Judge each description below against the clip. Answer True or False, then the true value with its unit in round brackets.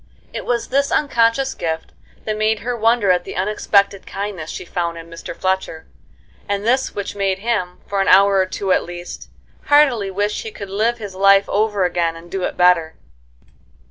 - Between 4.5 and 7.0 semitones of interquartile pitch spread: False (3.4 semitones)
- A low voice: False (200 Hz)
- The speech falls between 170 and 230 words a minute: True (185 wpm)